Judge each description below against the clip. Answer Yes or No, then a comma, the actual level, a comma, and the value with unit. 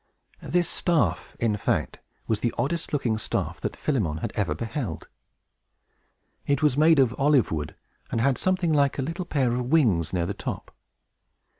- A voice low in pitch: Yes, low, 130 Hz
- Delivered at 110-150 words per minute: No, average, 165 wpm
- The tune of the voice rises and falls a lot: Yes, wide, 5.8 semitones